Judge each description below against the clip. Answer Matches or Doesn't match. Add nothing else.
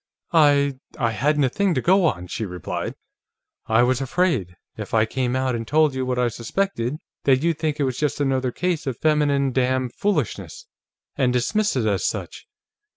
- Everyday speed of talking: Matches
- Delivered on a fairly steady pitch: Doesn't match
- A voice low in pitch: Matches